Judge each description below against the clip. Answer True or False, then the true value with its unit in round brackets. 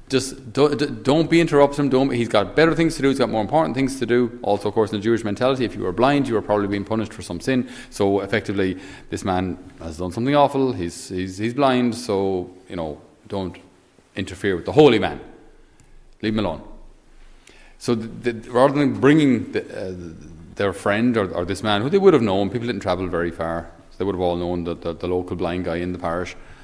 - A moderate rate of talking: False (230 wpm)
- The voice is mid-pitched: False (105 Hz)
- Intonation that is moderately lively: False (6.1 semitones)